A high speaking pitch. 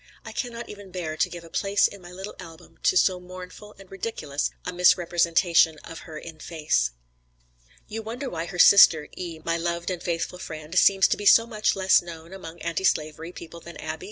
No: medium, 175 Hz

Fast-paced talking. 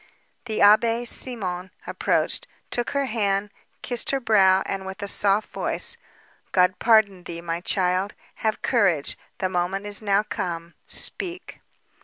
No: average, 140 wpm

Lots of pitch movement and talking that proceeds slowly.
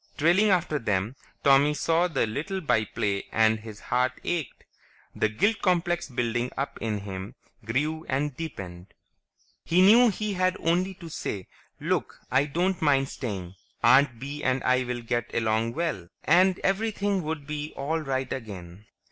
No: wide, 7.1 semitones; average, 155 wpm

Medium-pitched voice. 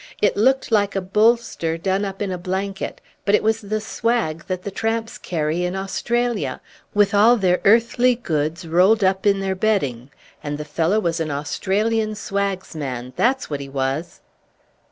No: high, 195 Hz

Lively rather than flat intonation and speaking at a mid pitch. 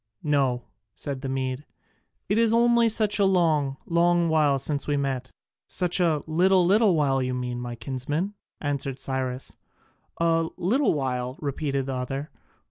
No: average, 4.8 semitones; medium, 145 Hz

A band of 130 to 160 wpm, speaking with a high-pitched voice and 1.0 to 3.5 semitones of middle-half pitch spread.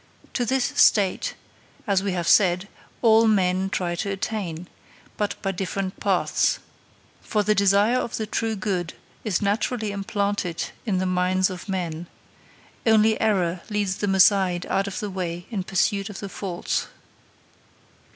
Yes: average, 150 wpm; high, 195 Hz; narrow, 2.5 semitones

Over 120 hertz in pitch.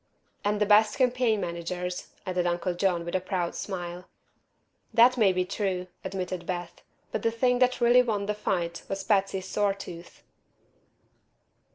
Yes: high, 190 Hz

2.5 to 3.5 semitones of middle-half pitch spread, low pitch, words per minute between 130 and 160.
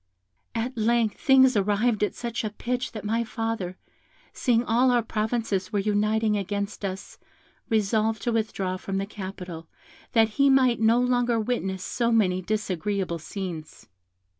No: average, 3.1 semitones; high, 215 Hz; average, 145 wpm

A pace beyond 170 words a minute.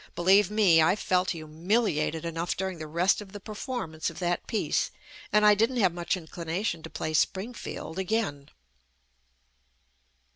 No: average, 145 wpm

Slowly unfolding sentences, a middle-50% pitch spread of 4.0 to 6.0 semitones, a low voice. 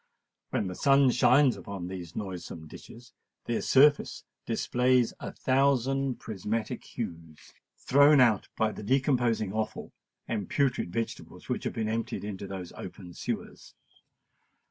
Yes: slow, 130 wpm; average, 5.2 semitones; low, 115 Hz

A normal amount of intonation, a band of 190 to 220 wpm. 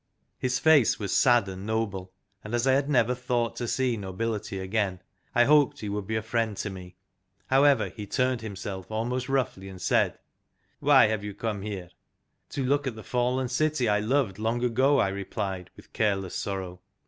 Yes: average, 4.3 semitones; average, 195 wpm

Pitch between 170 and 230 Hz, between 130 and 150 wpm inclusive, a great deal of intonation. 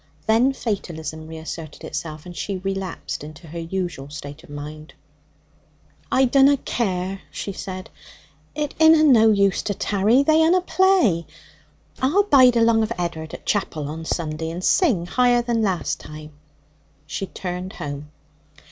Yes: high, 190 Hz; average, 145 wpm; wide, 7.2 semitones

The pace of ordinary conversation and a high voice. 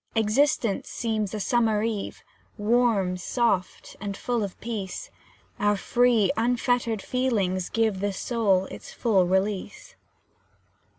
No: slow, 115 wpm; high, 215 Hz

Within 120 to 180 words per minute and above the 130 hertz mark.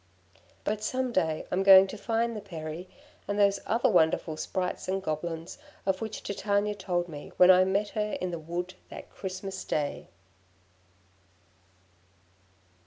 Yes: average, 145 wpm; high, 190 Hz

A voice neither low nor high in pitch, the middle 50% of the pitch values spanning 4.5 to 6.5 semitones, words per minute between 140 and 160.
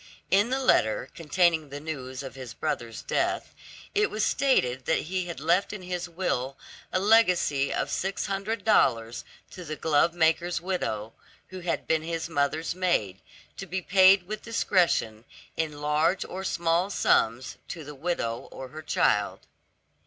Yes: medium, 165 Hz; average, 5.2 semitones; average, 155 wpm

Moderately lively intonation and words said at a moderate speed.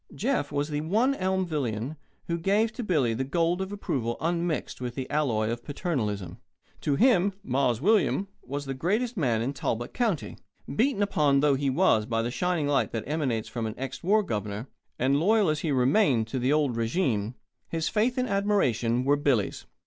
No: wide, 7.6 semitones; average, 185 wpm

